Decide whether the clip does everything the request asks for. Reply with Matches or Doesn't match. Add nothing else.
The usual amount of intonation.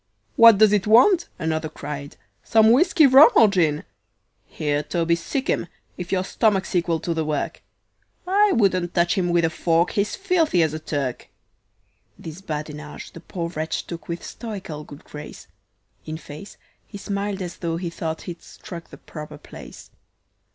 Matches